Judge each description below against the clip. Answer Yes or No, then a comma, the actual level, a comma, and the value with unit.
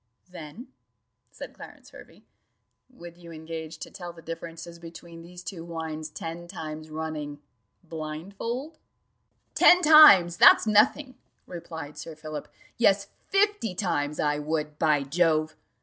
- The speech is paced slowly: Yes, slow, 130 wpm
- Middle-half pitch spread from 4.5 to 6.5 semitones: No, average, 2.9 semitones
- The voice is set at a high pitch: No, medium, 165 Hz